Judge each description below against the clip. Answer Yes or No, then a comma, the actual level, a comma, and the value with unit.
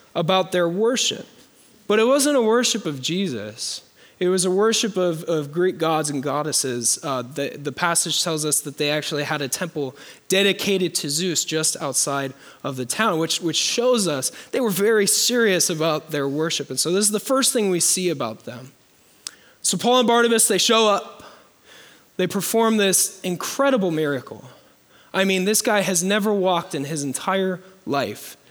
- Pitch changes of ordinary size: No, wide, 5.7 semitones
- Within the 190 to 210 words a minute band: No, average, 180 wpm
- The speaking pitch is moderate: Yes, medium, 180 Hz